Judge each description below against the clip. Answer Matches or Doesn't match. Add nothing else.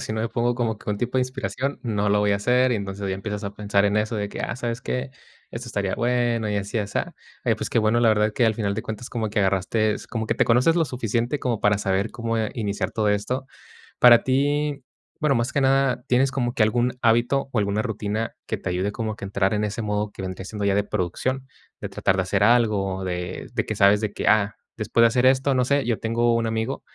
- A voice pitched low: Matches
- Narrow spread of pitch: Doesn't match